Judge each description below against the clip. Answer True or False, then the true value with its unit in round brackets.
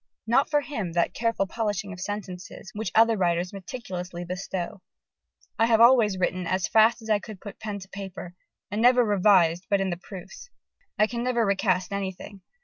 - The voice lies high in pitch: True (200 Hz)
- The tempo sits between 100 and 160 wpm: False (180 wpm)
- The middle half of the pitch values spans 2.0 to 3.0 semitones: False (3.4 semitones)